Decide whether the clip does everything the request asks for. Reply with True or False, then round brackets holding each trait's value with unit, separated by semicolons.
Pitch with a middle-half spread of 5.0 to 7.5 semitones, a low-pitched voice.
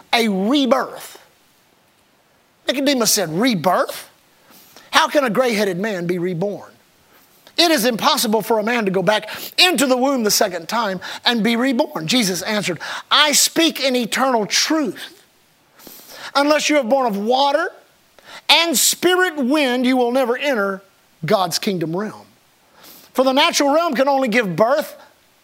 False (5.3 semitones; 255 Hz)